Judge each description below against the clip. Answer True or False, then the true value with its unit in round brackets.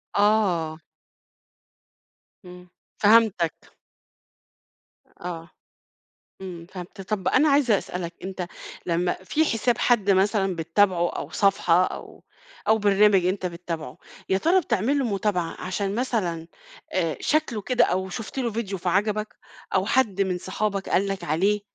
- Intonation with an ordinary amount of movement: True (3.1 semitones)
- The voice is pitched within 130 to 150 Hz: False (195 Hz)